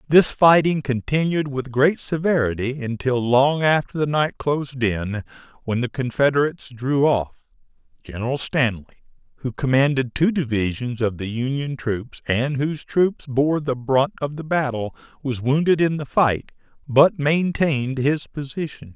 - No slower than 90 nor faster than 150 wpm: Yes, average, 145 wpm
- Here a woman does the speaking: No, male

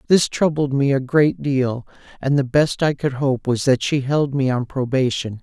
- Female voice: No, male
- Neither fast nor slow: No, fast, 210 wpm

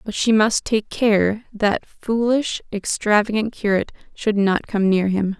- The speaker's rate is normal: Yes, average, 155 wpm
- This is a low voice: No, high, 210 Hz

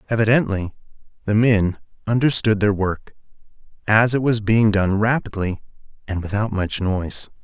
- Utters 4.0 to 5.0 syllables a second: Yes, 4.8 syllables/s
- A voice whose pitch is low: Yes, low, 105 Hz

